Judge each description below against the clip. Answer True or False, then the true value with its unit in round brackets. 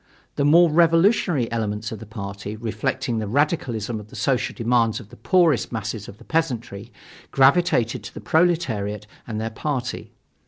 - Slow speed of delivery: False (160 wpm)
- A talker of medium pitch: False (120 Hz)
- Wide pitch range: True (5.7 semitones)